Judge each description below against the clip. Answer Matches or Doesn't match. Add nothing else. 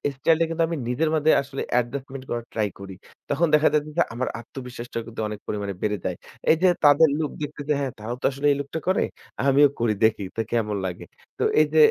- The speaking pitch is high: Doesn't match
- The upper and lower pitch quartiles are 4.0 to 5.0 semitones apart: Matches